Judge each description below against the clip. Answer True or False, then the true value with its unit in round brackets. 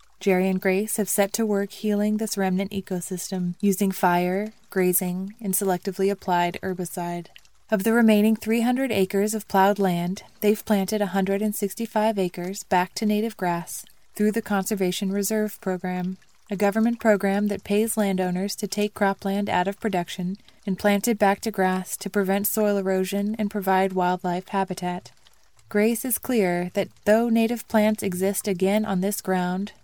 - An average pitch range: False (2.1 semitones)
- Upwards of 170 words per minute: False (155 wpm)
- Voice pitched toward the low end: False (200 Hz)